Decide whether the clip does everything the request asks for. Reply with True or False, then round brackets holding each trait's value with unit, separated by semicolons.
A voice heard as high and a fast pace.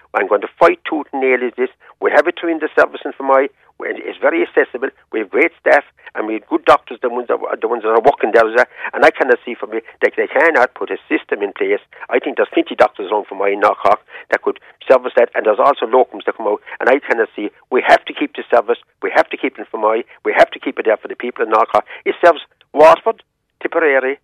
True (370 Hz; 260 wpm)